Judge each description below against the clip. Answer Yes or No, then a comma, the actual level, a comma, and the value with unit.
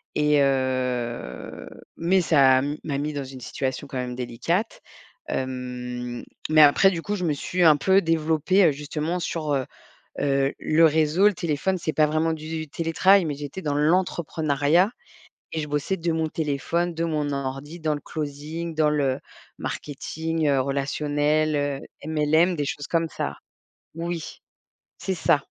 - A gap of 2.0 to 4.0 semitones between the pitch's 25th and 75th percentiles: Yes, average, 2.8 semitones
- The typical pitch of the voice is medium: Yes, medium, 150 Hz